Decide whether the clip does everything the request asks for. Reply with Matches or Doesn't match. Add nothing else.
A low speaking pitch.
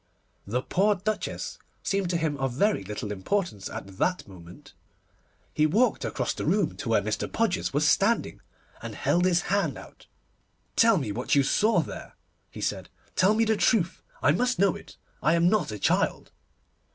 Doesn't match